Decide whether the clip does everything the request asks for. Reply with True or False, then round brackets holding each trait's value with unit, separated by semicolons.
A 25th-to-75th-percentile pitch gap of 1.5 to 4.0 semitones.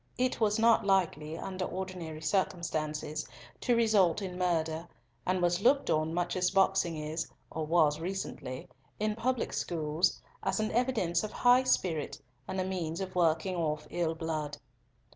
True (3.5 semitones)